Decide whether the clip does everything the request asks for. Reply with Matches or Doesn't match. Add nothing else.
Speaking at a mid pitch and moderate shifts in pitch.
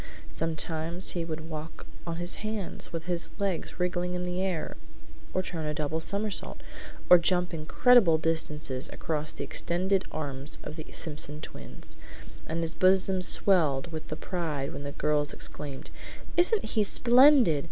Matches